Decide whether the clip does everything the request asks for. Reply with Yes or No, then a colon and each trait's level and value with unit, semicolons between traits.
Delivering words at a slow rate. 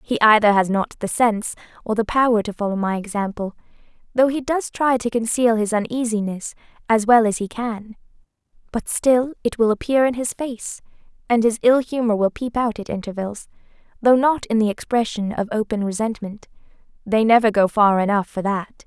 No: average, 180 wpm